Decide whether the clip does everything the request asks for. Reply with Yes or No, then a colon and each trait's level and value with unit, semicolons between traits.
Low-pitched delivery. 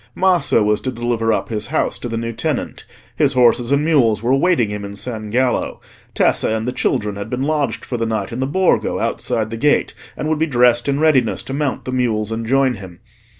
Yes: low, 120 Hz